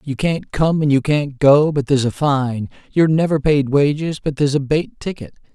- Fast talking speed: Yes, fast, 215 wpm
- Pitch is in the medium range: Yes, medium, 145 Hz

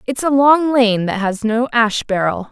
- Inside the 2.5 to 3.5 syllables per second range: No, 4.3 syllables/s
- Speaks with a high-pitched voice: Yes, high, 235 Hz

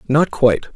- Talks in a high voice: No, low, 135 Hz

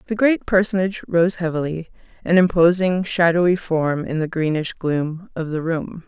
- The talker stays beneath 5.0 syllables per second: Yes, 4.8 syllables/s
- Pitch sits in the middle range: Yes, medium, 170 Hz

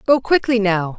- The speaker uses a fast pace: No, average, 185 wpm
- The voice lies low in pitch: No, high, 220 Hz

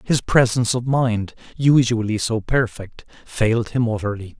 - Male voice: Yes, male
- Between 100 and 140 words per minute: Yes, slow, 135 wpm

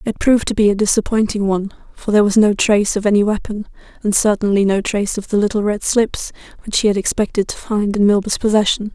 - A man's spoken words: No, female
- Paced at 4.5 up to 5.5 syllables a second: No, 6.4 syllables/s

